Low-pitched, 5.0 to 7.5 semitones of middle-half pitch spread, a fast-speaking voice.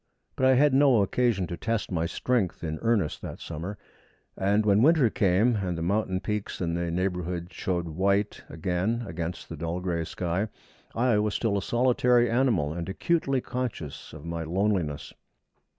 No: very low, 95 Hz; average, 5.3 semitones; average, 165 wpm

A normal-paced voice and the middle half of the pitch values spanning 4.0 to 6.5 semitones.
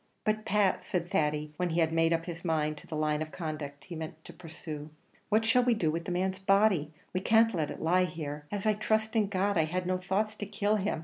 No: fast, 250 wpm; average, 4.5 semitones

